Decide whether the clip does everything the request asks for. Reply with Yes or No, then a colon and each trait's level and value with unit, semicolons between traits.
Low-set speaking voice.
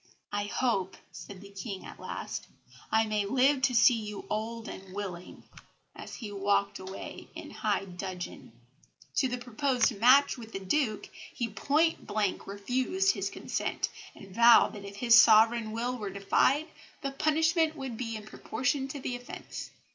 No: high, 225 Hz